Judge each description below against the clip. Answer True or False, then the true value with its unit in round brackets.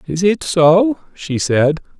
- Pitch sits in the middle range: True (175 Hz)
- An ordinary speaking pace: True (150 wpm)